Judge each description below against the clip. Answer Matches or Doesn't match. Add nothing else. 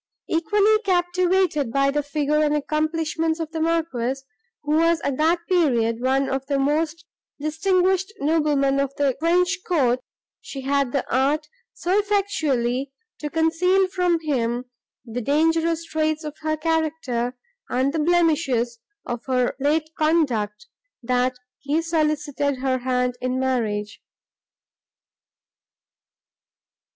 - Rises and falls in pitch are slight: Doesn't match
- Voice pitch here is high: Matches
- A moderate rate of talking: Doesn't match